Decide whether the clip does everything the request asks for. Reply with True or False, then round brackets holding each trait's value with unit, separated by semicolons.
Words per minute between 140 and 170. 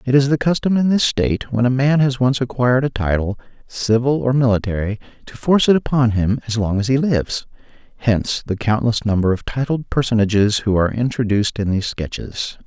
False (195 wpm)